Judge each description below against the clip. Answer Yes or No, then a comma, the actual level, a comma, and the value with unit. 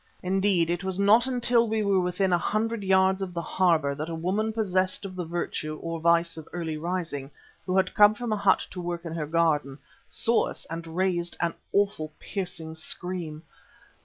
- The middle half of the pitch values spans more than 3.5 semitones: No, average, 3.0 semitones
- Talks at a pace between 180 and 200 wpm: Yes, average, 190 wpm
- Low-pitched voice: No, medium, 180 Hz